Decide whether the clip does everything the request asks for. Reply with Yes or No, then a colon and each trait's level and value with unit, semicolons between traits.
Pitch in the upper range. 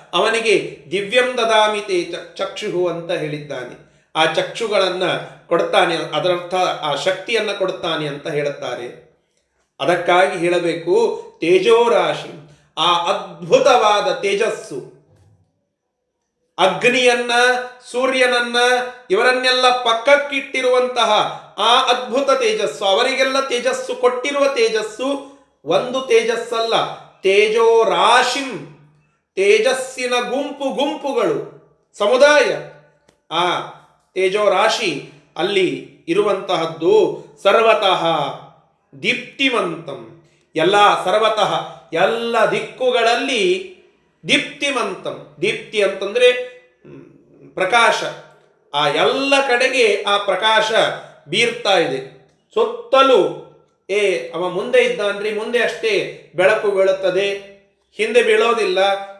Yes: high, 235 Hz